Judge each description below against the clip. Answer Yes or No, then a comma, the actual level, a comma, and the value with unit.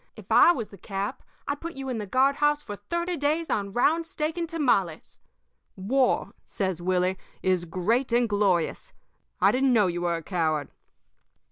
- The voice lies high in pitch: Yes, high, 225 Hz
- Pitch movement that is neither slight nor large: No, wide, 7.6 semitones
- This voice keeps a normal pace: Yes, average, 175 wpm